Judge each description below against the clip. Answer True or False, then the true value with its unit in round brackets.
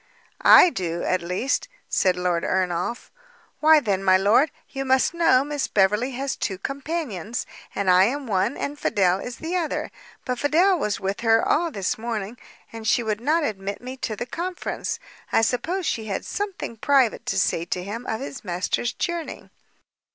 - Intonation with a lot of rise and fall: True (6.8 semitones)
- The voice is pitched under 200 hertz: False (230 Hz)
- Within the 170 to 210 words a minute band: True (175 wpm)